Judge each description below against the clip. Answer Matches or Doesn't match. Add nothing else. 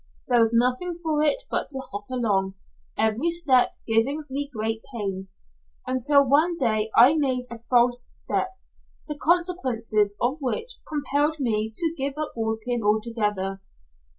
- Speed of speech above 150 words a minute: Doesn't match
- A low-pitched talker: Doesn't match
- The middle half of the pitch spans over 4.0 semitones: Matches